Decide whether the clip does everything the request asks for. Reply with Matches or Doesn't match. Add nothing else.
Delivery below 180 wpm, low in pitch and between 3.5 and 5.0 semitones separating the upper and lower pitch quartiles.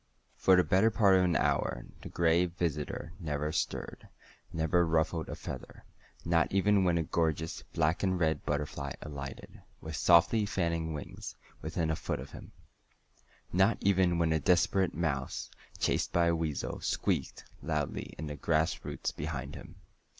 Doesn't match